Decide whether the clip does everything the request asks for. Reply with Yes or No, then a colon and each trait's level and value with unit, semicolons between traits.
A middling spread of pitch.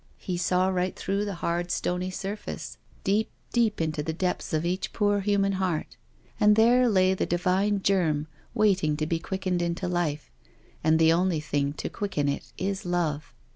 Yes: average, 3.2 semitones